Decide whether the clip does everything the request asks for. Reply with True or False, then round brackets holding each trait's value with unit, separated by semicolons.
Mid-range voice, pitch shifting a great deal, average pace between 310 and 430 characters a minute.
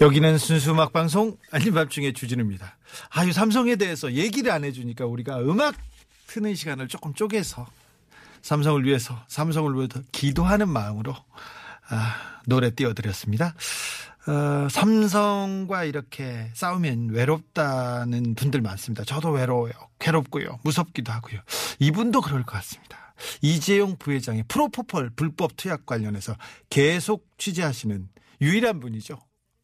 True (145 Hz; 6.1 semitones; 325 characters per minute)